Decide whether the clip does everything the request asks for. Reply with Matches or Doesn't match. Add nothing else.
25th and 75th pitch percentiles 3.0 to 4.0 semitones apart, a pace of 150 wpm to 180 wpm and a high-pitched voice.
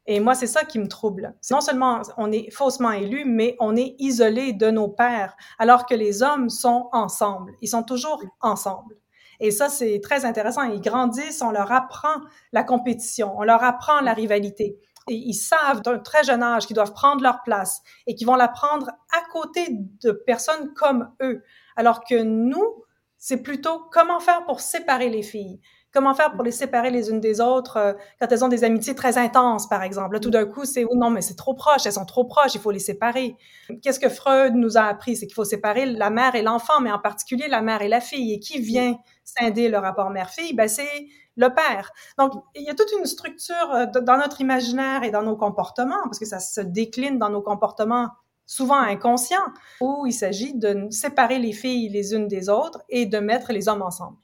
Doesn't match